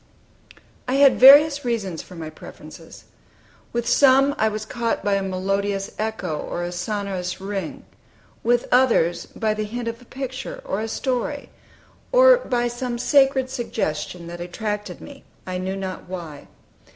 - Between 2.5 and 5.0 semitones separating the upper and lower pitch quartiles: No, wide, 5.6 semitones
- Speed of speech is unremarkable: Yes, average, 150 wpm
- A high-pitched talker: Yes, high, 220 Hz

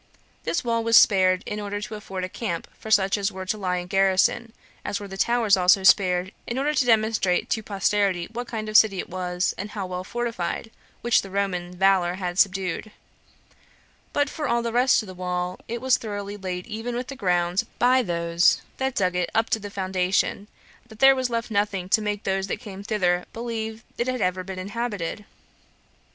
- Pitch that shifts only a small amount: No, average, 3.7 semitones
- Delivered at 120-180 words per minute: No, fast, 205 wpm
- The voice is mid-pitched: No, high, 200 Hz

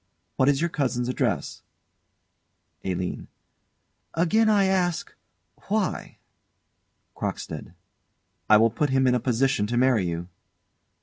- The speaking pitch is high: No, low, 130 Hz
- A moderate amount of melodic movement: No, wide, 6.9 semitones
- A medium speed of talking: No, slow, 115 wpm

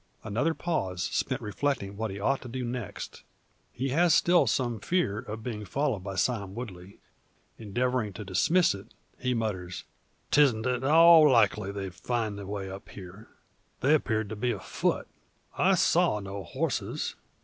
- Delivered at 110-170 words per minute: Yes, average, 160 wpm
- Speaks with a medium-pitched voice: No, low, 110 Hz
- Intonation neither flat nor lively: Yes, average, 4.7 semitones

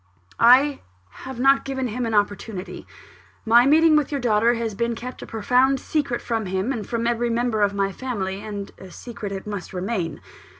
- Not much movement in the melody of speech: No, average, 3.7 semitones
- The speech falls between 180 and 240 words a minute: Yes, average, 185 wpm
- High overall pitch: Yes, high, 230 Hz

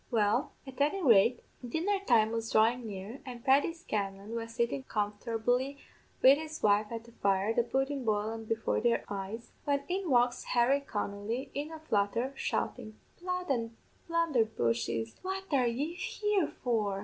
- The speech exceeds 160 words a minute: No, average, 155 wpm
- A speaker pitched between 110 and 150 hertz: No, high, 235 Hz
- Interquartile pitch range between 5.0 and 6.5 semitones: No, average, 4.5 semitones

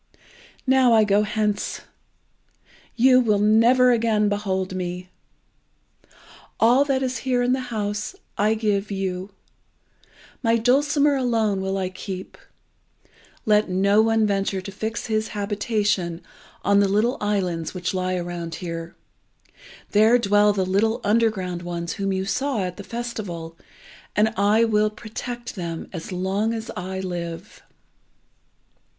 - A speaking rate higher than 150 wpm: No, slow, 135 wpm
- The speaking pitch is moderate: No, high, 205 Hz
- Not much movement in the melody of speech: No, average, 3.3 semitones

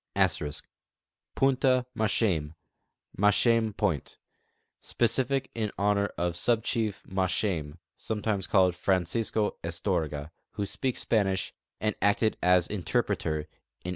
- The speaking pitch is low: Yes, low, 100 Hz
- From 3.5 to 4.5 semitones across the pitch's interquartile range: Yes, average, 4.2 semitones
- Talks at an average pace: No, slow, 110 wpm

